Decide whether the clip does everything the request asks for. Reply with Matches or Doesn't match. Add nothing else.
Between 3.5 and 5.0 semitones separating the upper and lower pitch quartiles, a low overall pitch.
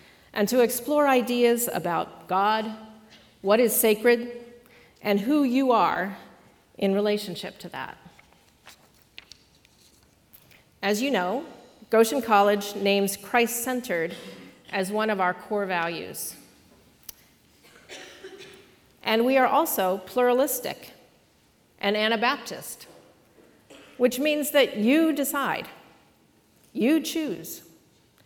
Doesn't match